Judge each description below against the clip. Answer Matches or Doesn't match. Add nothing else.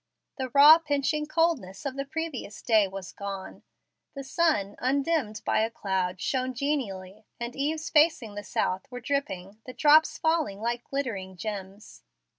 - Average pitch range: Doesn't match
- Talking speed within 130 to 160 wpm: Matches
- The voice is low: Doesn't match